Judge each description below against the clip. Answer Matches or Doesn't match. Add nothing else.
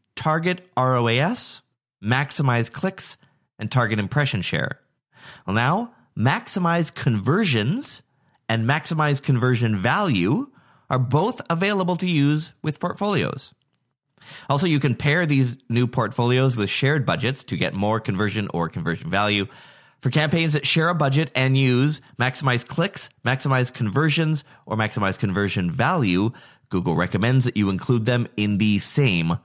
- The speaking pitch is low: Matches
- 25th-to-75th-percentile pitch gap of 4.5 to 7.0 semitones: Matches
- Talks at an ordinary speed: Doesn't match